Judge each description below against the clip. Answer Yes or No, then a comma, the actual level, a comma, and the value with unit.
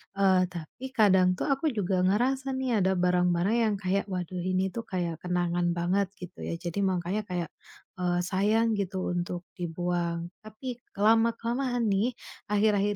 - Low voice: No, high, 190 Hz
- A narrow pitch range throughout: No, average, 3.4 semitones